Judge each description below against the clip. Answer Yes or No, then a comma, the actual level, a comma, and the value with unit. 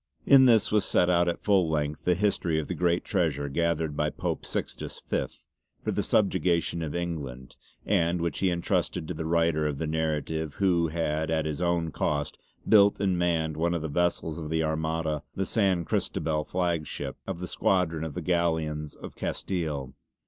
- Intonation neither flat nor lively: No, narrow, 2.3 semitones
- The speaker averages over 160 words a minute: Yes, average, 185 wpm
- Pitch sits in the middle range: No, very low, 80 Hz